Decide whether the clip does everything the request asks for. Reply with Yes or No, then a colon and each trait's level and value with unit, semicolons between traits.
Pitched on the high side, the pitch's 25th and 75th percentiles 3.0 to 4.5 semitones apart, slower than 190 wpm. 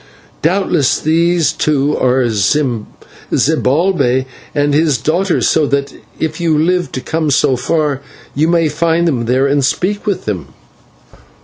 No: medium, 150 Hz; average, 4.0 semitones; slow, 135 wpm